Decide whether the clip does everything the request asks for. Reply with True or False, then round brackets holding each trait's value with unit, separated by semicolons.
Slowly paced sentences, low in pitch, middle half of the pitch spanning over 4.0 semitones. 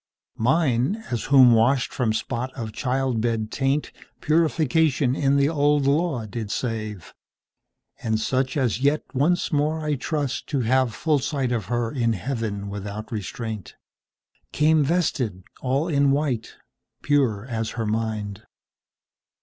True (120 wpm; 130 Hz; 4.4 semitones)